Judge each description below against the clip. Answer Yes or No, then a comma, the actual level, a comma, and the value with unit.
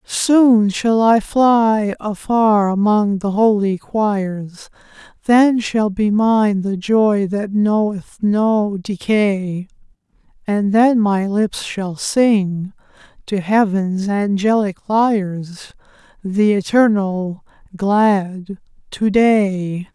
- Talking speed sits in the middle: No, slow, 100 wpm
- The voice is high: Yes, high, 205 Hz